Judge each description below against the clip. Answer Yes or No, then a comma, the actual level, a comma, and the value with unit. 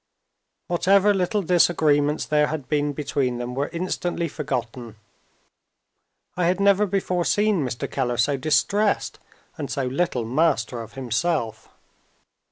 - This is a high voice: No, medium, 150 Hz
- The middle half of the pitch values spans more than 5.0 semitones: Yes, wide, 5.6 semitones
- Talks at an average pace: No, slow, 125 wpm